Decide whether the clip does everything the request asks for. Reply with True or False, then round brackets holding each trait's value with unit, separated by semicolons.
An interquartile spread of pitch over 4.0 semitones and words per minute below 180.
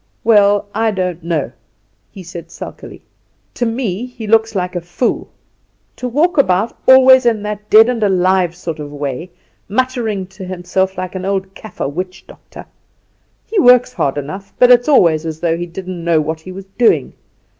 True (4.5 semitones; 170 wpm)